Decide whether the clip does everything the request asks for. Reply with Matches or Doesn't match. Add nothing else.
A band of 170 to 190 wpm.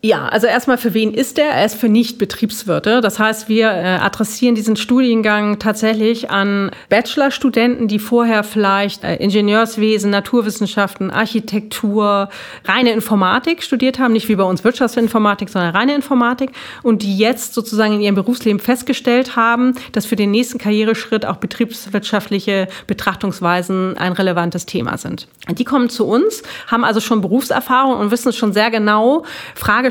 Doesn't match